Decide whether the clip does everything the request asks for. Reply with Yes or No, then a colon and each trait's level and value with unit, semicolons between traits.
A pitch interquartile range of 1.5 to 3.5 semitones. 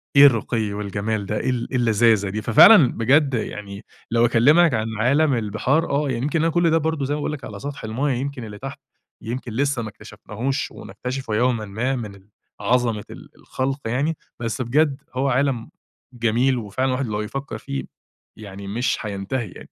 No: average, 4.1 semitones